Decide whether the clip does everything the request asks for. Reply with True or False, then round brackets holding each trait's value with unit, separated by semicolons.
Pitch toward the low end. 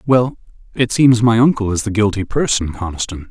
True (110 Hz)